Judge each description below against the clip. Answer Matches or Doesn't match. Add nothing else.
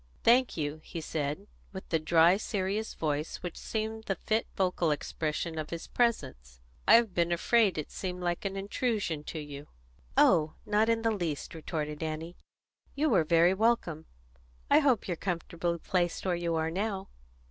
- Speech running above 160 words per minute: Matches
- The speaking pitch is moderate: Matches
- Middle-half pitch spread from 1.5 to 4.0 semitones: Doesn't match